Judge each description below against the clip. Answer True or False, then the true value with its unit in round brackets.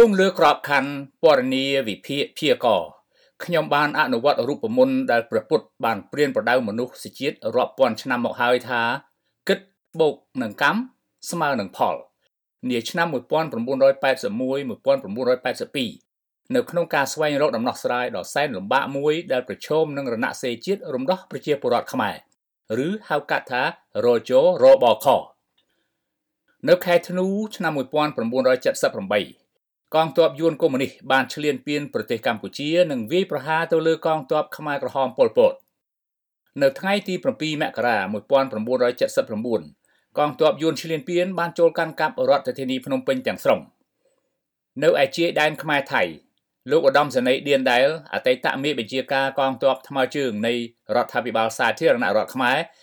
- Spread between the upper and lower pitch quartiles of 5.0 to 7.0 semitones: True (5.4 semitones)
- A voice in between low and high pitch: True (155 Hz)